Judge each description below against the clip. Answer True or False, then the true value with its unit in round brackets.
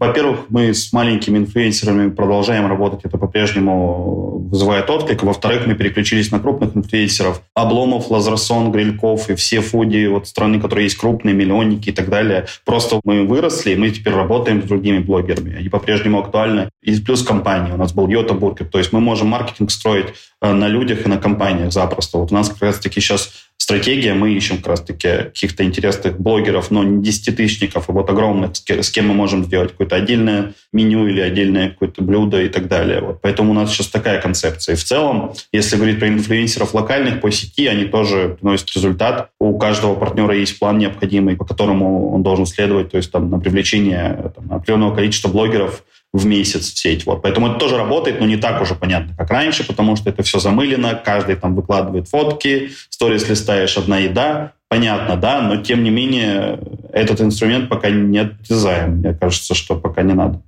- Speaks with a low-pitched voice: True (105 Hz)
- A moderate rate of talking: False (185 wpm)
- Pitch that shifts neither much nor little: False (1.9 semitones)